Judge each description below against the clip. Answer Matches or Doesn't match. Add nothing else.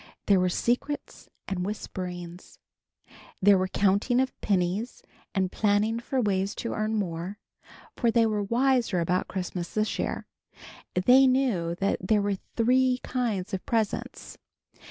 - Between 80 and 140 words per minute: Matches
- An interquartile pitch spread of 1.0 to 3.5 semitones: Doesn't match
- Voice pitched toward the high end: Matches